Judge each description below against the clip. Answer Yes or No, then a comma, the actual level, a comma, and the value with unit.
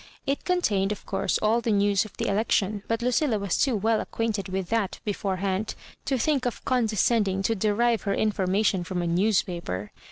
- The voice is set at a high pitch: Yes, high, 210 Hz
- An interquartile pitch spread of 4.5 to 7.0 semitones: No, average, 3.0 semitones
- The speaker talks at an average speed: Yes, average, 185 wpm